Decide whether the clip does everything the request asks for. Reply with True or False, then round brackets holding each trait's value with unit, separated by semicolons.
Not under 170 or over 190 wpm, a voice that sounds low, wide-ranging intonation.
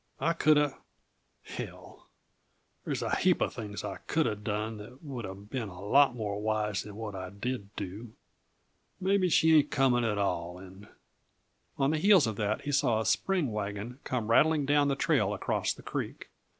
True (180 wpm; 115 Hz; 5.7 semitones)